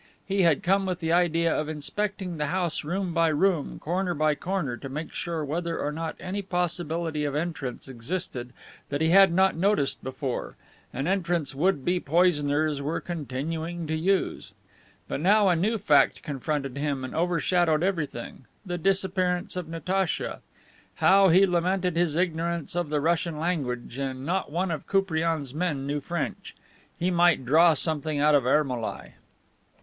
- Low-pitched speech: No, medium, 165 Hz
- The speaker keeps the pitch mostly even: No, average, 3.5 semitones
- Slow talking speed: No, average, 160 wpm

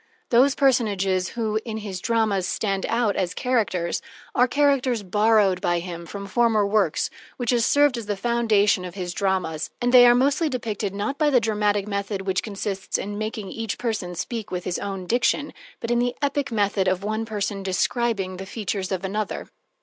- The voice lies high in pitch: Yes, high, 210 Hz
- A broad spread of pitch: No, average, 3.6 semitones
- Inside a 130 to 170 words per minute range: No, average, 185 wpm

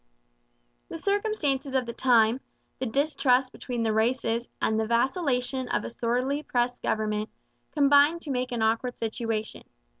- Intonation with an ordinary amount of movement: Yes, average, 3.2 semitones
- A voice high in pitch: Yes, very high, 250 Hz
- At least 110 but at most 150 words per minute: Yes, average, 145 wpm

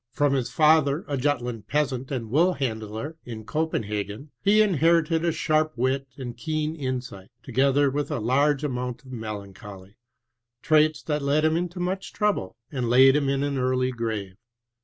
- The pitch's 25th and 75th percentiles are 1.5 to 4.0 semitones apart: No, average, 4.5 semitones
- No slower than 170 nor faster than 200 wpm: No, average, 160 wpm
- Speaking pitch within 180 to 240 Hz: No, low, 135 Hz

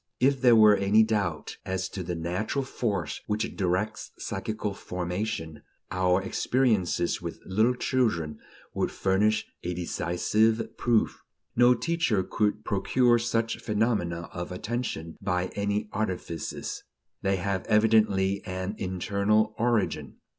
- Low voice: Yes, low, 100 Hz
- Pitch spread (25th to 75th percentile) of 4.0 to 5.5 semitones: No, average, 3.3 semitones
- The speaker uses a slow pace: Yes, slow, 120 wpm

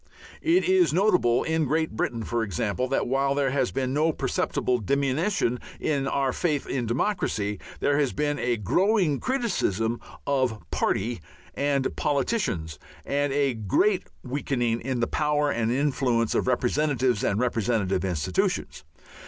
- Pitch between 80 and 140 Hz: Yes, low, 135 Hz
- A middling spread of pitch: Yes, average, 4.1 semitones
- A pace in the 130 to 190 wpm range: Yes, average, 140 wpm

